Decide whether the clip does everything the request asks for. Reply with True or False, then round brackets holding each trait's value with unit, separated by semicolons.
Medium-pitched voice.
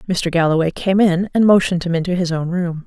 True (175 Hz)